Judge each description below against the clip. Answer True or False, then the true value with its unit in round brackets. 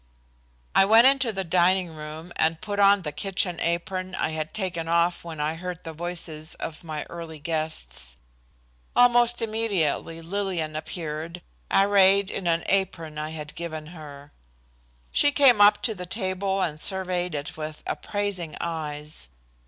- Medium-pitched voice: True (170 Hz)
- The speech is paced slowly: False (150 wpm)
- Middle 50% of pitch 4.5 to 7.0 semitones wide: False (3.7 semitones)